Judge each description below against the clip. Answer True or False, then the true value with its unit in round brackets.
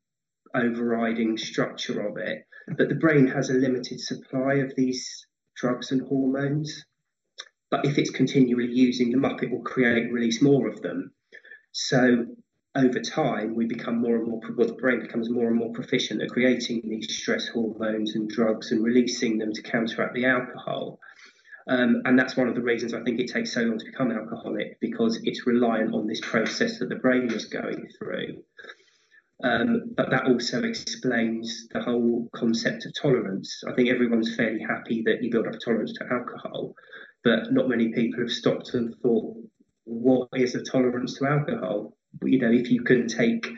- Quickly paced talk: False (180 wpm)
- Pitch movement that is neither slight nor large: False (2.0 semitones)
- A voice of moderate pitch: False (120 Hz)